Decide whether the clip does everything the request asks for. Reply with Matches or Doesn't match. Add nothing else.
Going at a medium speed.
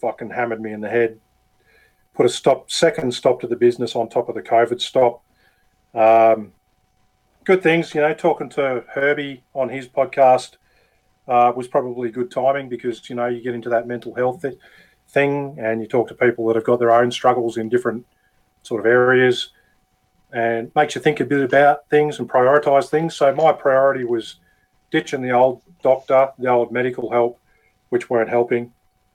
Matches